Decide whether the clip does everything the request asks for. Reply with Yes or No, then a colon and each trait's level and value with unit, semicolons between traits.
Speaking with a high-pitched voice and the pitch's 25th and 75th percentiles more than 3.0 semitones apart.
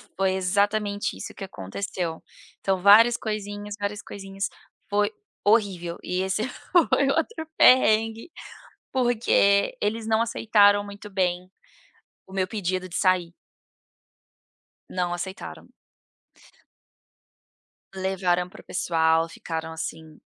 No: high, 195 Hz; average, 2.7 semitones